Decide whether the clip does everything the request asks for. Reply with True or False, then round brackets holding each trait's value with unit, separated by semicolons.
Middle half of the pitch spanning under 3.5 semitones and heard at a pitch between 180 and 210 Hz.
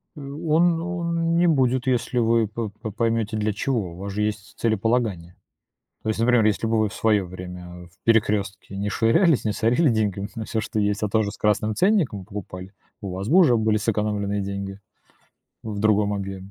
False (2.9 semitones; 110 Hz)